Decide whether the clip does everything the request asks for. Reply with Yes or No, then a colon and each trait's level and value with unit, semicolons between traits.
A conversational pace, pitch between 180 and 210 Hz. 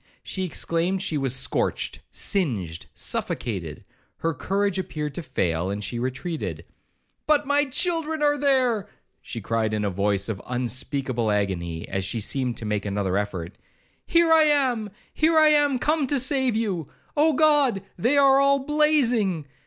Yes: average, 150 wpm; medium, 185 Hz